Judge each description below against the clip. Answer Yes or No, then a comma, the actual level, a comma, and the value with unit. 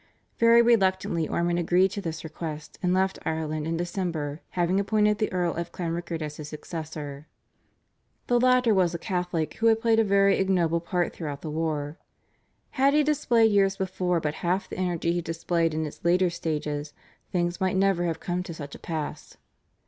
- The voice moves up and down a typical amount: Yes, average, 3.3 semitones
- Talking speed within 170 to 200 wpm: Yes, average, 180 wpm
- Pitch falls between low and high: Yes, medium, 175 Hz